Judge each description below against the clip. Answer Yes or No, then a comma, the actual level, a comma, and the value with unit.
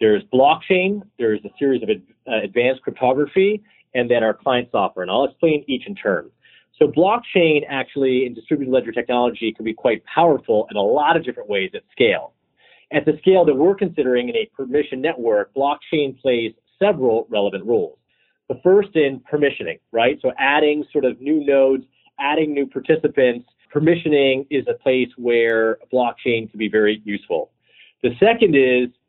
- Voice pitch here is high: No, medium, 140 Hz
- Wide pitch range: Yes, wide, 6.4 semitones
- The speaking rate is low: No, average, 165 wpm